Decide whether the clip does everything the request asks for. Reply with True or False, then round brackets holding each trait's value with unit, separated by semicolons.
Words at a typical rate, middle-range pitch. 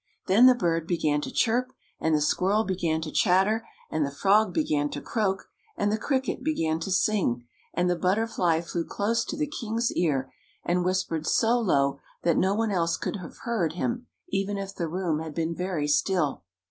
True (190 wpm; 180 Hz)